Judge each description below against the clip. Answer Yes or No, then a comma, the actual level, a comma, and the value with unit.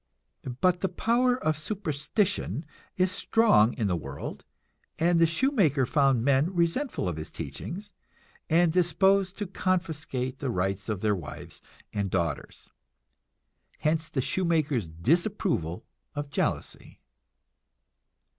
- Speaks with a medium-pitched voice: Yes, medium, 160 Hz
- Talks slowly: Yes, slow, 115 wpm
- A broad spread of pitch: Yes, wide, 7.4 semitones